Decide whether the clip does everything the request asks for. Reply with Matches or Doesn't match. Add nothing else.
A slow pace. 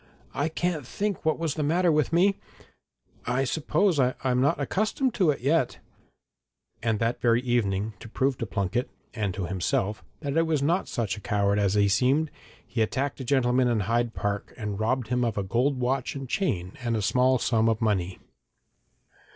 Doesn't match